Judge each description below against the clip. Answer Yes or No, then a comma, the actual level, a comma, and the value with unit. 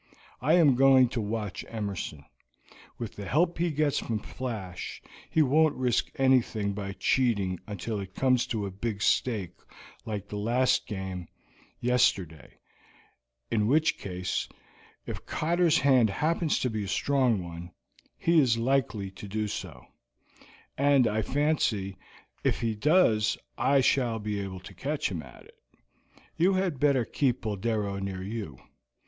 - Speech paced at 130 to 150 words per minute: Yes, average, 145 wpm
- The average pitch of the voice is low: Yes, low, 115 Hz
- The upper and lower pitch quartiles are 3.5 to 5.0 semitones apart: No, wide, 5.4 semitones